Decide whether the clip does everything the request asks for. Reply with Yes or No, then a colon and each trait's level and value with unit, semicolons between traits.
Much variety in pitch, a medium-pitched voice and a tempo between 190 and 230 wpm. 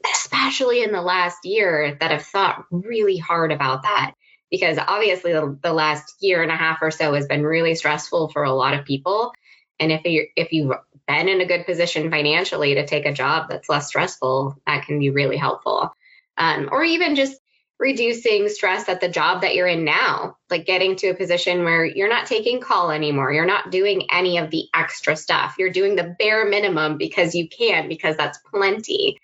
Yes: wide, 5.9 semitones; medium, 175 Hz; average, 200 wpm